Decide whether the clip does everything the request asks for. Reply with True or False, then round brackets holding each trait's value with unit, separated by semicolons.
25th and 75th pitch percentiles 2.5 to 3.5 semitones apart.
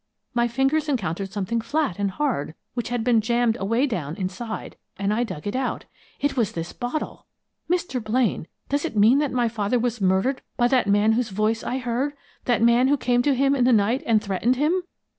False (3.9 semitones)